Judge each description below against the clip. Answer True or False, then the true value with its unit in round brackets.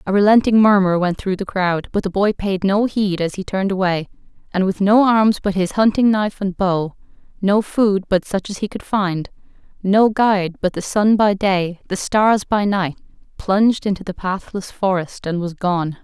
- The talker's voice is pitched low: False (195 Hz)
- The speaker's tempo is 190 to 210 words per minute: True (200 wpm)